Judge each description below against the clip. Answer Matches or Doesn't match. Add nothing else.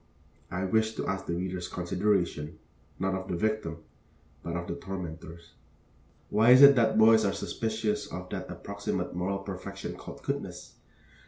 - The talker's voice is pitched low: Matches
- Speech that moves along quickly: Doesn't match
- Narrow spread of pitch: Doesn't match